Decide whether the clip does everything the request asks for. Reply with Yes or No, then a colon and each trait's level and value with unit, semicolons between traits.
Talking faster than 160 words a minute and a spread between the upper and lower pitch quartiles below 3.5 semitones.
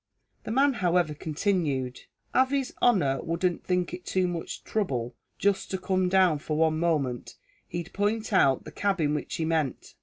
No: average, 170 wpm; average, 4.3 semitones